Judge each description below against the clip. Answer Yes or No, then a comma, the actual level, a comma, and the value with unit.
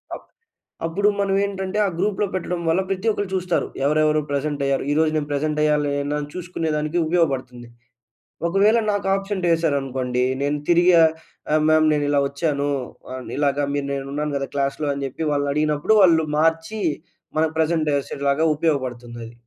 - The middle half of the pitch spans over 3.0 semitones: Yes, average, 3.6 semitones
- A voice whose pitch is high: No, medium, 155 Hz